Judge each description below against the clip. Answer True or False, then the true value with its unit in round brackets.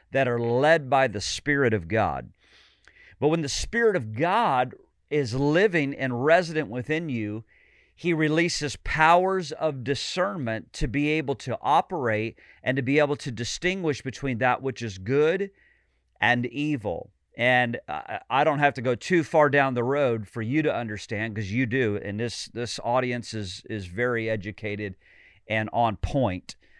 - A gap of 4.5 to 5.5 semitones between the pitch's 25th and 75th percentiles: True (5.1 semitones)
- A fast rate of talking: False (160 wpm)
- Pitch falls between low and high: False (130 Hz)